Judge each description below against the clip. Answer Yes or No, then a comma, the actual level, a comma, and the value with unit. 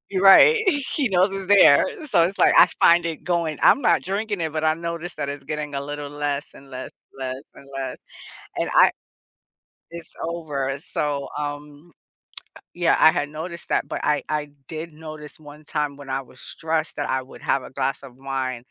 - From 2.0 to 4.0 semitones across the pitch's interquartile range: Yes, average, 3.2 semitones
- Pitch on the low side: No, medium, 150 Hz